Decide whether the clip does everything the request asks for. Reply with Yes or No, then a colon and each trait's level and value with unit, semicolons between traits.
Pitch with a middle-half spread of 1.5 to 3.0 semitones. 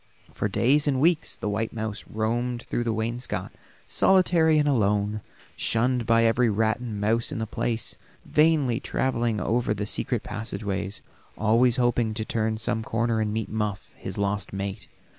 Yes: narrow, 2.4 semitones